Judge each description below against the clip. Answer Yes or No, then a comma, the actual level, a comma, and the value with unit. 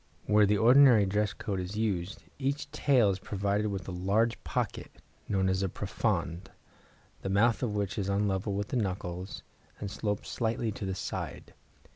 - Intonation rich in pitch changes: No, narrow, 2.5 semitones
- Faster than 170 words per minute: Yes, average, 180 wpm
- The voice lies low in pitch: Yes, low, 100 Hz